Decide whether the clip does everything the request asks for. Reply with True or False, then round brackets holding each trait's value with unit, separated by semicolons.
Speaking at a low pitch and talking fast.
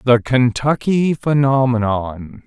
False (125 Hz; 75 wpm)